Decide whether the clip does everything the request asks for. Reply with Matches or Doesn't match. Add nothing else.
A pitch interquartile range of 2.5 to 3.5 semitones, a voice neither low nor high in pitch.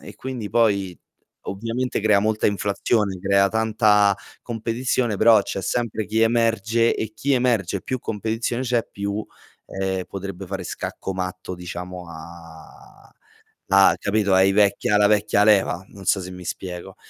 Doesn't match